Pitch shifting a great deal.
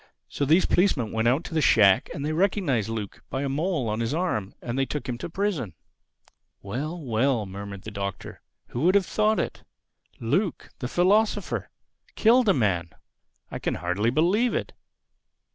Yes: wide, 8.7 semitones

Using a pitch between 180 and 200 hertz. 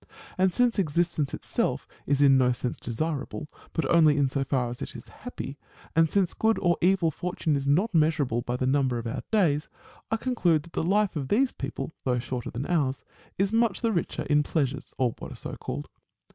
No: medium, 155 Hz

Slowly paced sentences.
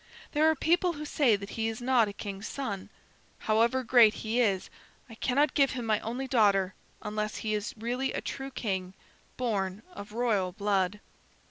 No: average, 175 wpm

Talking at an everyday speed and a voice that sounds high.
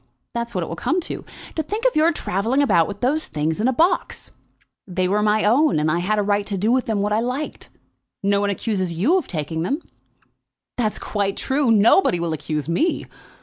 No: fast, 210 wpm; high, 210 Hz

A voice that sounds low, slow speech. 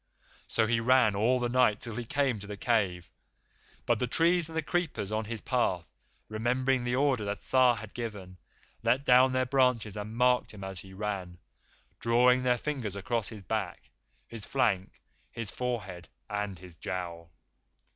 No: low, 115 Hz; average, 170 wpm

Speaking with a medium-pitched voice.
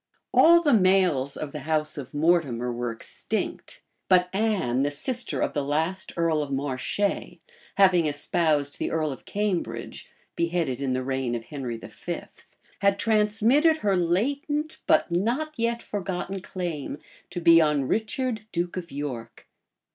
Yes: medium, 170 Hz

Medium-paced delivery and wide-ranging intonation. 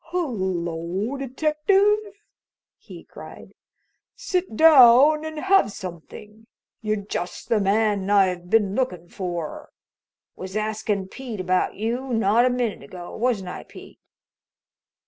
No: slow, 115 wpm; wide, 5.9 semitones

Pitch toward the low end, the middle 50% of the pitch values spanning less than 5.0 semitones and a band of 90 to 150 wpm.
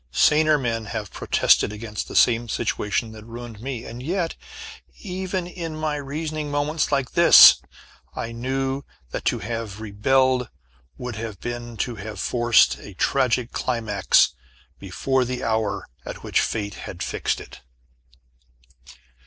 Yes: low, 120 Hz; average, 4.4 semitones; slow, 135 wpm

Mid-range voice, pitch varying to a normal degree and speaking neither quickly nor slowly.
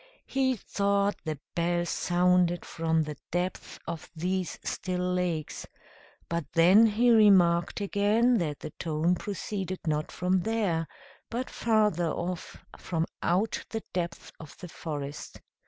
No: medium, 180 Hz; average, 3.4 semitones; slow, 130 wpm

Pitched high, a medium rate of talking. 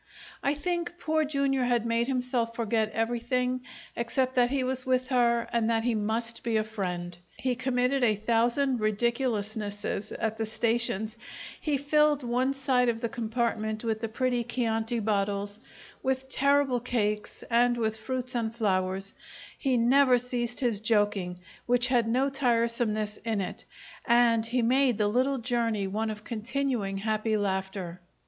Yes: high, 235 Hz; average, 155 wpm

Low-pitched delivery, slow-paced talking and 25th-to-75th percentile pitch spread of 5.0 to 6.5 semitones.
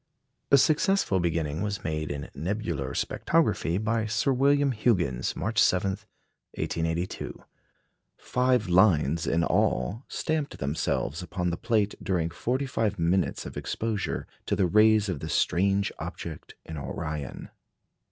Yes: very low, 95 Hz; slow, 130 wpm; average, 5.3 semitones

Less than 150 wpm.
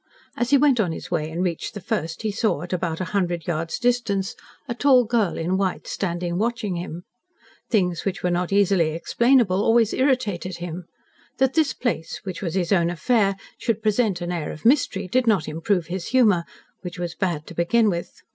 No: average, 195 wpm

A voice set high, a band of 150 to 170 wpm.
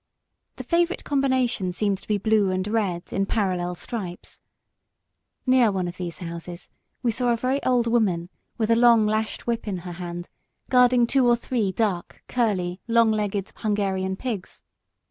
Yes: high, 210 Hz; average, 165 wpm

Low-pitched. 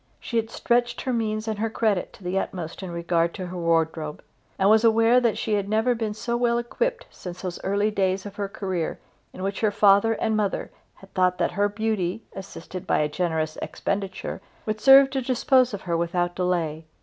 No: high, 200 Hz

